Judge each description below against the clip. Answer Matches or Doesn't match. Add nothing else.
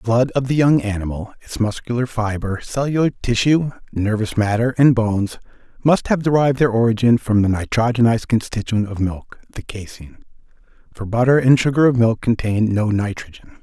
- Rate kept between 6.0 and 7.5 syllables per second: Doesn't match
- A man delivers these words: Matches